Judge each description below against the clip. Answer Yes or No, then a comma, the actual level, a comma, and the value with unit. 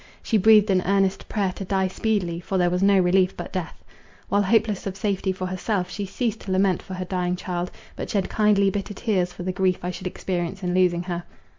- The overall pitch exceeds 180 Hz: Yes, high, 190 Hz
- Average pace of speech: No, fast, 225 wpm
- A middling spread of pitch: No, narrow, 1.7 semitones